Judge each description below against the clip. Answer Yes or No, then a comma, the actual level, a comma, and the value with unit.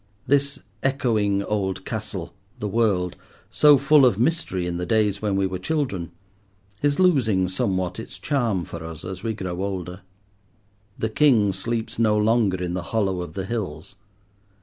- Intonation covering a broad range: No, average, 4.1 semitones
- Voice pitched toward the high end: No, low, 100 Hz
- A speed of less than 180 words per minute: Yes, average, 160 wpm